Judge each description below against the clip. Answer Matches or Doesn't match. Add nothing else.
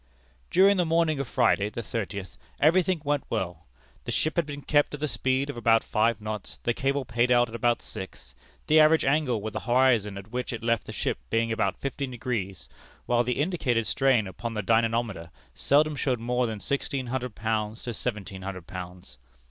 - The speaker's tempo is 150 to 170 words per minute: Doesn't match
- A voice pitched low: Matches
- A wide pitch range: Doesn't match